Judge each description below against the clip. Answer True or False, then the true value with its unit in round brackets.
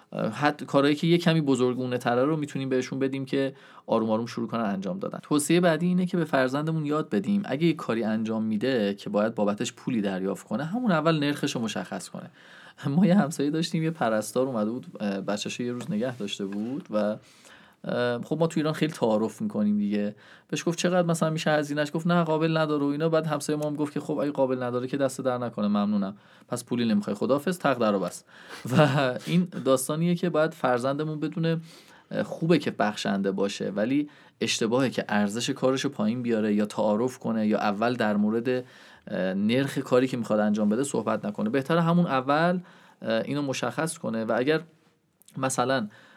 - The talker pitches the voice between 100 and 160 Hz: True (140 Hz)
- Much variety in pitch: True (6.2 semitones)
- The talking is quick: True (185 wpm)